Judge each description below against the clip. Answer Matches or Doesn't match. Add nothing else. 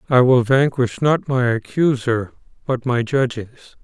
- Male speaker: Matches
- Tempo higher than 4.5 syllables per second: Doesn't match